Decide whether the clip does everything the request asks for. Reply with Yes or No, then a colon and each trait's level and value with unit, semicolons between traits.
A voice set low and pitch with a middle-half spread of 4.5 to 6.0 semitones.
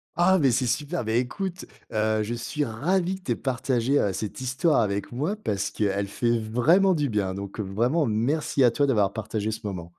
Yes: low, 120 Hz; wide, 5.6 semitones